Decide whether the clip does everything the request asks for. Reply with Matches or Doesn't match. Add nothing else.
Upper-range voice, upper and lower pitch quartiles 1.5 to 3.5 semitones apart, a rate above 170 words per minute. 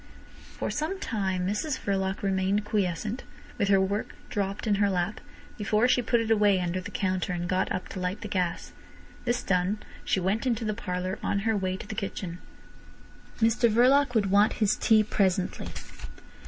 Matches